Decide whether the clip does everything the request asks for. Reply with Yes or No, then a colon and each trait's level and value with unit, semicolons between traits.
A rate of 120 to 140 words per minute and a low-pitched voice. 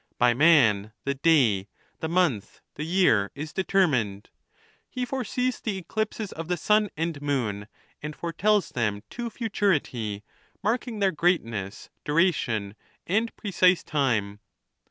No: slow, 135 wpm; medium, 160 Hz